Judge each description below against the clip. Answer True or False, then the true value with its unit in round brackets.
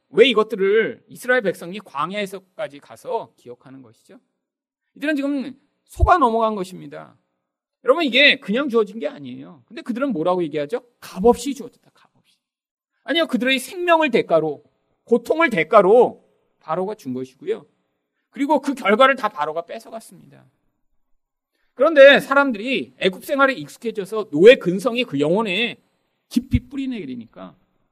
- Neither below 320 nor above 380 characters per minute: True (335 characters per minute)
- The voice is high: True (230 Hz)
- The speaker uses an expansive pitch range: True (7.9 semitones)